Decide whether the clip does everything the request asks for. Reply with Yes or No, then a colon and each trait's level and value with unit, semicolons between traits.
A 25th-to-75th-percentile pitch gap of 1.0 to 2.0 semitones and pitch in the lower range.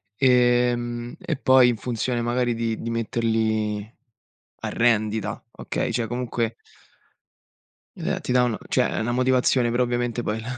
Yes: narrow, 1.5 semitones; low, 120 Hz